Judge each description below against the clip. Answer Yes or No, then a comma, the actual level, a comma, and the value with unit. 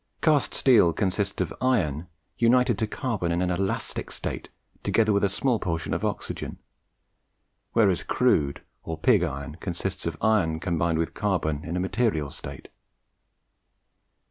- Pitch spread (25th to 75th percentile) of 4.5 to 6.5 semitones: Yes, average, 5.1 semitones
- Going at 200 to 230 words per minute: No, average, 145 wpm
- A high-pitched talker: No, very low, 90 Hz